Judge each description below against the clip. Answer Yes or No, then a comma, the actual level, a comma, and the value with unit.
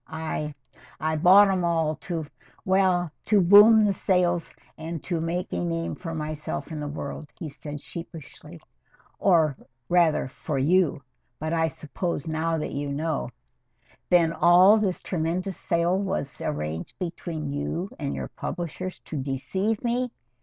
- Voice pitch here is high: No, medium, 165 Hz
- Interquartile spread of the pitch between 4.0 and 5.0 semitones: No, average, 3.1 semitones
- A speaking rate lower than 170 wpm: Yes, average, 150 wpm